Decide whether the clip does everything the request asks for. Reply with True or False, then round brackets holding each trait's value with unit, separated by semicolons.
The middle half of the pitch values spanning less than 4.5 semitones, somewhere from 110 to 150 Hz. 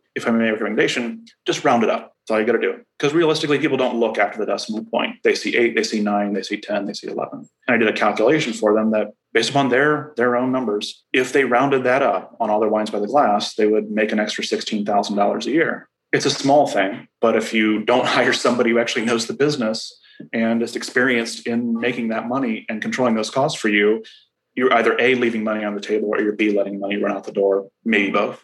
True (2.9 semitones; 115 Hz)